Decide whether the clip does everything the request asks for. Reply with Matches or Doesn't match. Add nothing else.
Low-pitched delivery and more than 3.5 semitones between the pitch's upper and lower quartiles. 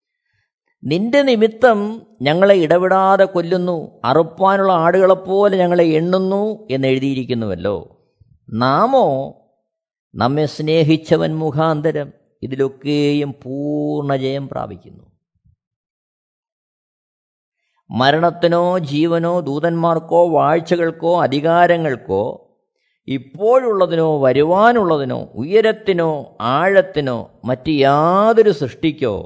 Doesn't match